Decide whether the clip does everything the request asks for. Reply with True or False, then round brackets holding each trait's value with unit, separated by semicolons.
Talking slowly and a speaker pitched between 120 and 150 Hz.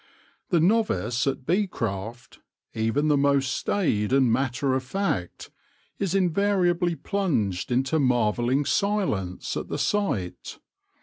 True (120 wpm; 135 Hz)